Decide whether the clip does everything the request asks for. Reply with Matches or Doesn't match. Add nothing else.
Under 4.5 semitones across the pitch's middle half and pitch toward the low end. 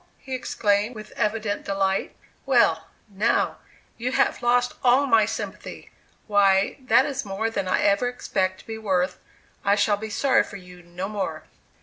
Doesn't match